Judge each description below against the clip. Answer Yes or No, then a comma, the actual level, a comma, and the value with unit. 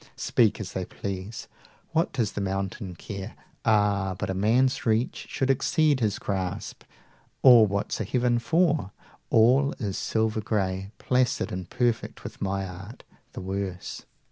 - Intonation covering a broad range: No, average, 4.1 semitones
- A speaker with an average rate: Yes, average, 150 wpm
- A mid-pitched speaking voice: No, low, 105 Hz